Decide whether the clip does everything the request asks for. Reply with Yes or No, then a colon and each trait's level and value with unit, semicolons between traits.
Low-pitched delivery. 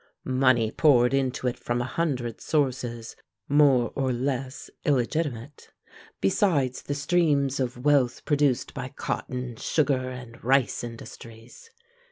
Yes: low, 130 Hz